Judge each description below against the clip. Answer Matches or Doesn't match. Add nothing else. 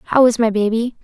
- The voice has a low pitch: Doesn't match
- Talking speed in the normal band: Doesn't match